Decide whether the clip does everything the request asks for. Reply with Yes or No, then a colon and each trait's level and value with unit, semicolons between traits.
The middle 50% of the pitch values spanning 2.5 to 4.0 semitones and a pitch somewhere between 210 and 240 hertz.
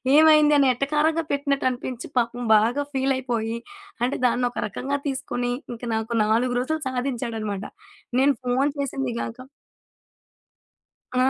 No: average, 2.9 semitones; very high, 255 Hz